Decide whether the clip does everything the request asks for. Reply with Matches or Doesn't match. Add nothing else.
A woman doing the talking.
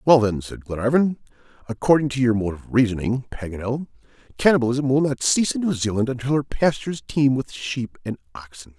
Doesn't match